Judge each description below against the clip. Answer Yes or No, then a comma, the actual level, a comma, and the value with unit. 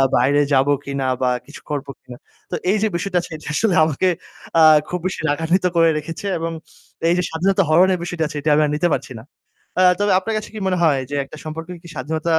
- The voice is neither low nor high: Yes, medium, 160 Hz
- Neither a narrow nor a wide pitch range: Yes, average, 3.6 semitones